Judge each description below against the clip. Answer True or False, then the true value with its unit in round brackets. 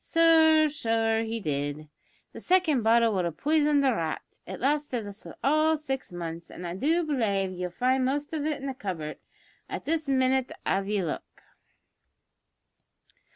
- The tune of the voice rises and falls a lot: True (7.7 semitones)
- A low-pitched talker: False (250 Hz)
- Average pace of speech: True (165 wpm)